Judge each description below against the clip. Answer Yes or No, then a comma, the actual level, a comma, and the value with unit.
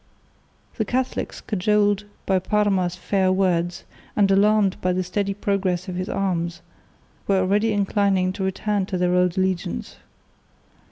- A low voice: No, high, 190 Hz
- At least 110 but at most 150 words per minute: Yes, slow, 135 wpm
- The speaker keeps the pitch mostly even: Yes, narrow, 2.0 semitones